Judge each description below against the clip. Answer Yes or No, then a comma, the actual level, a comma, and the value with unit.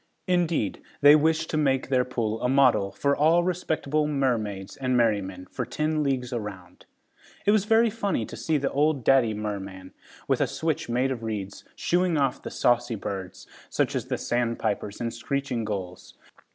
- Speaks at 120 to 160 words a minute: No, average, 170 wpm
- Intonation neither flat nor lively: No, wide, 6.2 semitones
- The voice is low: Yes, low, 125 Hz